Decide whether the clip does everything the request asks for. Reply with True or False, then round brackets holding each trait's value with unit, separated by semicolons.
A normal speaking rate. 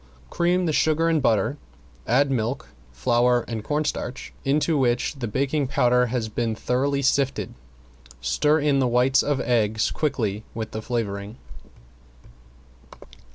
False (130 wpm)